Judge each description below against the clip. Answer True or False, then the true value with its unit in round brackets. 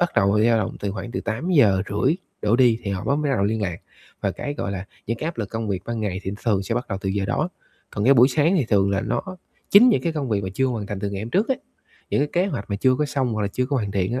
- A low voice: True (110 Hz)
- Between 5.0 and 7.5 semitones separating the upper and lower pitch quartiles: True (5.3 semitones)